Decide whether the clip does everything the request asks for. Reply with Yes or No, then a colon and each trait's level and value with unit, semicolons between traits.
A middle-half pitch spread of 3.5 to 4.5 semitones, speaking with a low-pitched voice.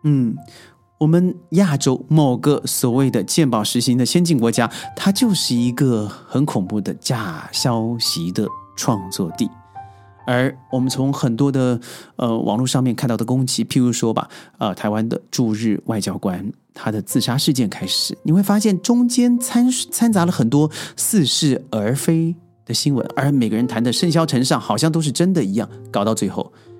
No: wide, 5.5 semitones; low, 130 Hz